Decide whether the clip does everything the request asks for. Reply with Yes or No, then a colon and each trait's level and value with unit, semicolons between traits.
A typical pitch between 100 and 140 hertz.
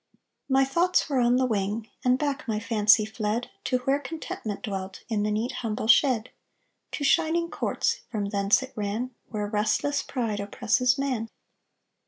No: high, 230 Hz